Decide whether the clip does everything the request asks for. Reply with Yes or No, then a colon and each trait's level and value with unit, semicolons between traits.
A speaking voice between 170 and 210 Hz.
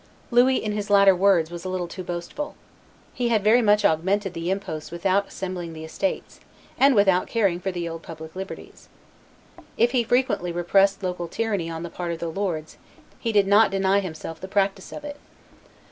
Yes: high, 190 Hz